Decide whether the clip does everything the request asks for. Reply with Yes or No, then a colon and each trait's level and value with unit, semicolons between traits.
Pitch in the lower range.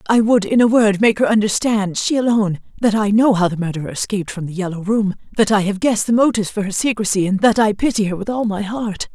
No: high, 210 Hz